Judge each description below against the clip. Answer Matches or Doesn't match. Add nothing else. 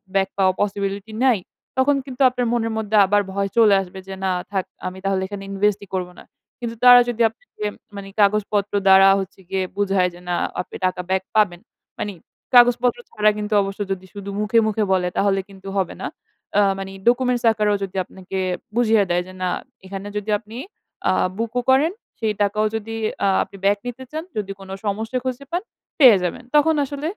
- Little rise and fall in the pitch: Doesn't match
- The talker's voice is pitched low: Doesn't match